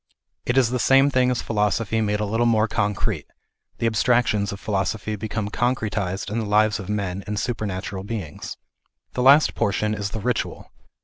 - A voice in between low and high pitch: No, low, 105 Hz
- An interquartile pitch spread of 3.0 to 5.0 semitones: No, narrow, 2.5 semitones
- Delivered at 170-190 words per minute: Yes, average, 175 wpm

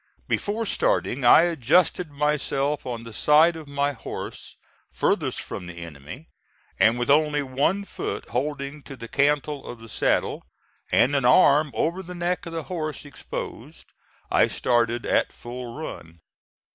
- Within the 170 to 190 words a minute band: No, average, 150 wpm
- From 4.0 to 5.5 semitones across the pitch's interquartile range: Yes, average, 4.4 semitones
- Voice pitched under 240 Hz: Yes, medium, 140 Hz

